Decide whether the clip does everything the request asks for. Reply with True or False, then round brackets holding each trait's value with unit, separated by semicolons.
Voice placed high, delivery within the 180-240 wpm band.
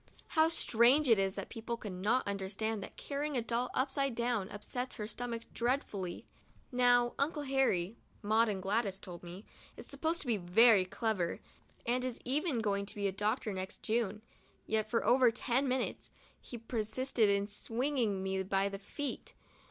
False (225 Hz; 165 wpm)